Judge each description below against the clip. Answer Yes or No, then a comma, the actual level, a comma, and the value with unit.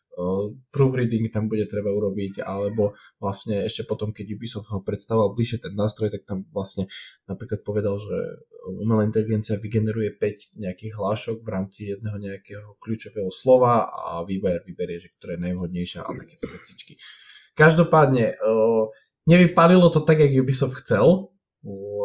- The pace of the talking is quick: No, average, 145 wpm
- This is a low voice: Yes, low, 105 Hz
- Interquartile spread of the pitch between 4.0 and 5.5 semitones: No, narrow, 2.4 semitones